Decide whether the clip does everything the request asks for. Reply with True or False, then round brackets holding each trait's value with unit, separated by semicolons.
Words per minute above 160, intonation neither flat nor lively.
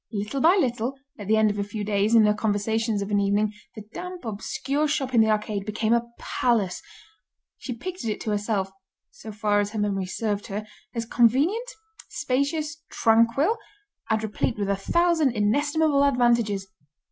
True (170 wpm; 4.8 semitones)